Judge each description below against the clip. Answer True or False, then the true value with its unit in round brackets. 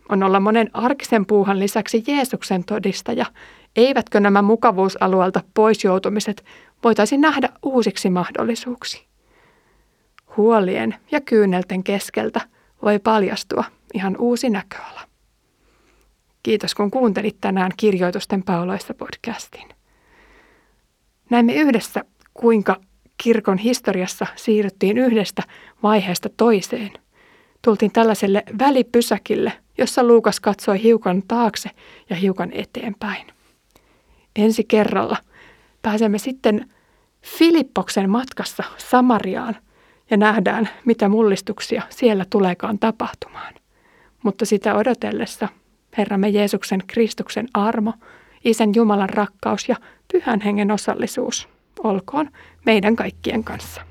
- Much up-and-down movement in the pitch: False (2.7 semitones)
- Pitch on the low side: False (220 Hz)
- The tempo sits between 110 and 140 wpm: False (95 wpm)